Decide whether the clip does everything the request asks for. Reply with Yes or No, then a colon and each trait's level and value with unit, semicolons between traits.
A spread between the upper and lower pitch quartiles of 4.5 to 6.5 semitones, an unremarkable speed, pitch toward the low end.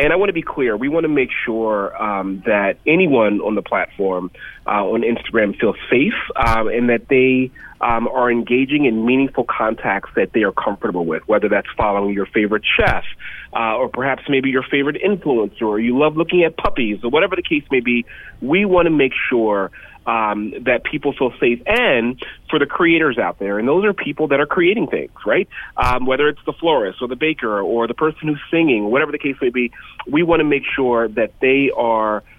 No: average, 5.2 semitones; fast, 210 wpm; low, 125 Hz